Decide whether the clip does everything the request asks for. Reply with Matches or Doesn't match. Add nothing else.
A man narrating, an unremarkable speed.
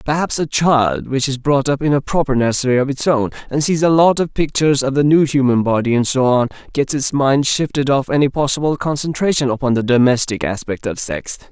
Doesn't match